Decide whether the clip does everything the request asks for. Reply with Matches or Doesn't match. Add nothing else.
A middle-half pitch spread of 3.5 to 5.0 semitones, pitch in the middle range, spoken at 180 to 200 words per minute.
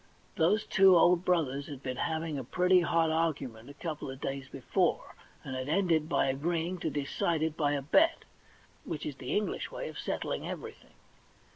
Matches